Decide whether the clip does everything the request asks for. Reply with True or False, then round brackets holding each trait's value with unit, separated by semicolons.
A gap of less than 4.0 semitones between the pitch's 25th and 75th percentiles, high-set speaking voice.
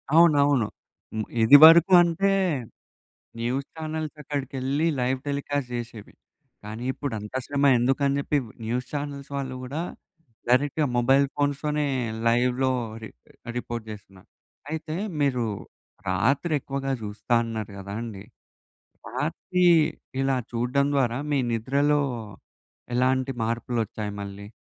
False (3.5 semitones; 135 Hz)